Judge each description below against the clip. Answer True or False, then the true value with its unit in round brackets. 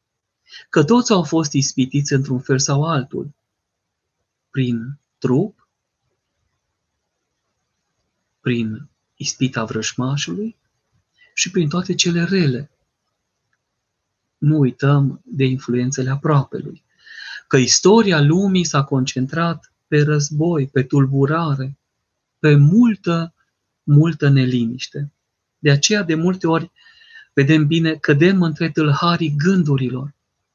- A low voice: False (145 Hz)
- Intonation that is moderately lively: True (4.3 semitones)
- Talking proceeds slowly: True (95 wpm)